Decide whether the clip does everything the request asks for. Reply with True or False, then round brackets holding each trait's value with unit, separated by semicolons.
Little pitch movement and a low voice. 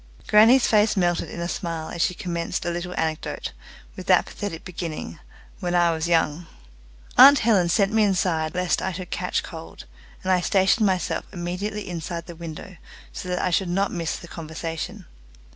False (2.3 semitones; 175 Hz)